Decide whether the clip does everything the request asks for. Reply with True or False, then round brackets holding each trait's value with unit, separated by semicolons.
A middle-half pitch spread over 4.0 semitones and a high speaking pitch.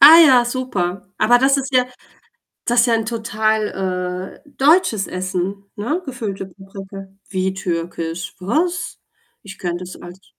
True (4.7 semitones; 200 Hz)